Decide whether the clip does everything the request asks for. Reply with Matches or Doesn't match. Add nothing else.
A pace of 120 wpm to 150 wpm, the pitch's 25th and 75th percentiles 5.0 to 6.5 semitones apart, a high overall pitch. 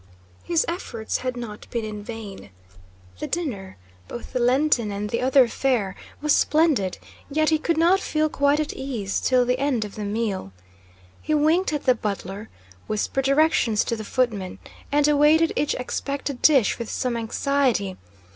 Doesn't match